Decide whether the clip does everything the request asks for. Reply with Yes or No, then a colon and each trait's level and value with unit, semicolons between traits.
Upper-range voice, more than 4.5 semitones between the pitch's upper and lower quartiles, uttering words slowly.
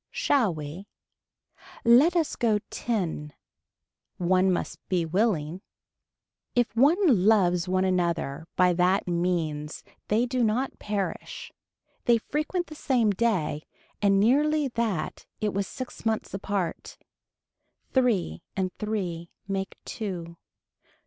Yes: high, 195 Hz; average, 5.1 semitones; slow, 115 wpm